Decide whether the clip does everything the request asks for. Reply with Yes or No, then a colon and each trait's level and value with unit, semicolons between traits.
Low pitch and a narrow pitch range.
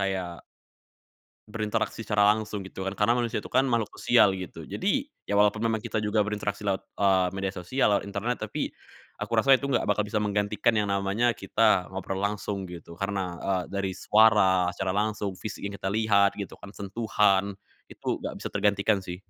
Yes: low, 100 Hz; narrow, 1.9 semitones